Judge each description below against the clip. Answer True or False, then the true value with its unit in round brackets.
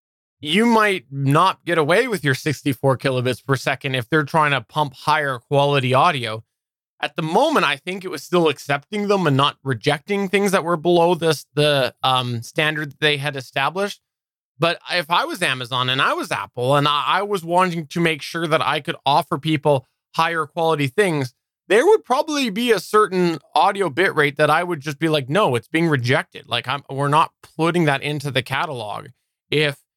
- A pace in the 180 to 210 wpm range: True (190 wpm)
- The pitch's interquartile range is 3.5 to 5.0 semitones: True (3.9 semitones)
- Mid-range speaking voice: True (155 Hz)